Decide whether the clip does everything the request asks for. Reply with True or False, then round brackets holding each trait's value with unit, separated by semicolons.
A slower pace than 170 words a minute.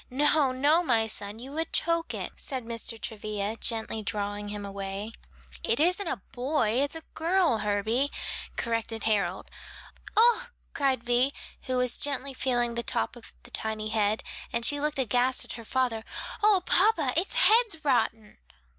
True (160 wpm)